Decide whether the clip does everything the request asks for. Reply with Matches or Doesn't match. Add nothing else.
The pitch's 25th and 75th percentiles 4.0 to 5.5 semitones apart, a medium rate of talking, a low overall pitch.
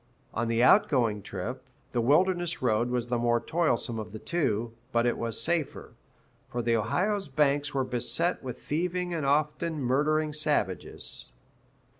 Matches